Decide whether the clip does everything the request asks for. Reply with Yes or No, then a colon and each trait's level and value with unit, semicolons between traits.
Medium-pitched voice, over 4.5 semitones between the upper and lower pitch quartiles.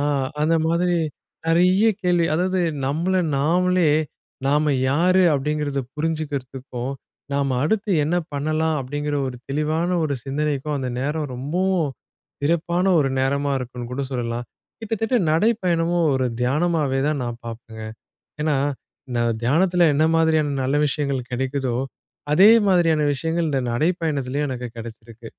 No: medium, 150 Hz; average, 4.0 semitones